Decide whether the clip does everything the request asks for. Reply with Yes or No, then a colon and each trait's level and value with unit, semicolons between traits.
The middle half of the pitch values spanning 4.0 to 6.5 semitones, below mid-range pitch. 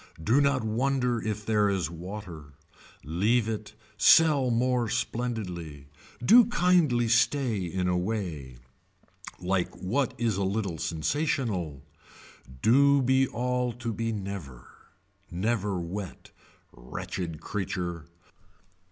Yes: wide, 5.6 semitones; low, 105 Hz